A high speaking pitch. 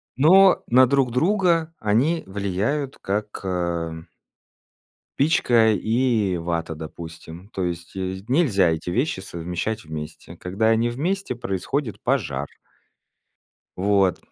No: low, 105 Hz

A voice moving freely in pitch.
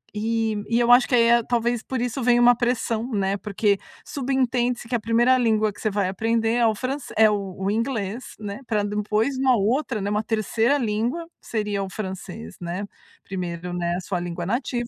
No: average, 3.2 semitones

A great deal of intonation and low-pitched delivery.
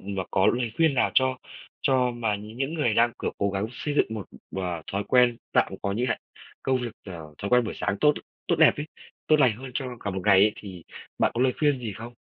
No: average, 4.4 semitones; low, 115 Hz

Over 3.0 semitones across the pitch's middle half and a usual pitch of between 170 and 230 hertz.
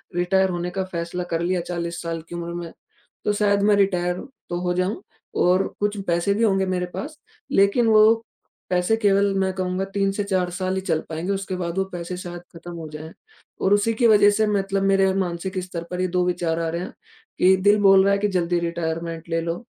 No: narrow, 2.4 semitones; medium, 185 Hz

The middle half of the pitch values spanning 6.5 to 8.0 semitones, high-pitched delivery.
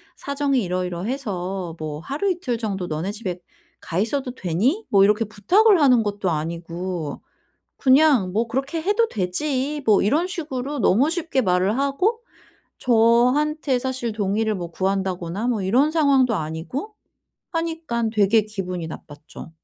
Yes: wide, 7.2 semitones; high, 225 Hz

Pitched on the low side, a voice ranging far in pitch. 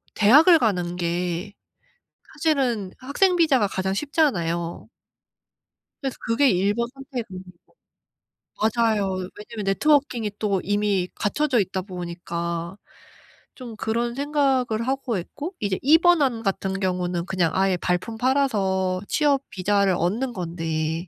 No: high, 205 Hz; wide, 6.3 semitones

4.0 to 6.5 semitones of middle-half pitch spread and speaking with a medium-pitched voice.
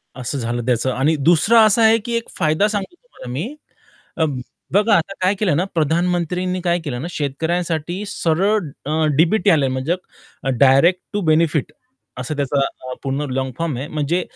Yes: average, 4.6 semitones; medium, 160 Hz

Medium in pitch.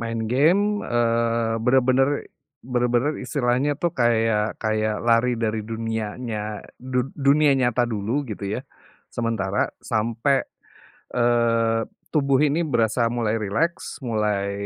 No: low, 115 Hz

